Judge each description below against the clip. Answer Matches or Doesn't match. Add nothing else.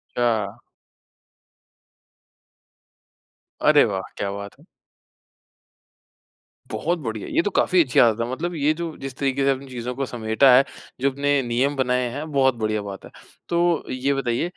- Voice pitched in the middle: Doesn't match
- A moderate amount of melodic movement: Matches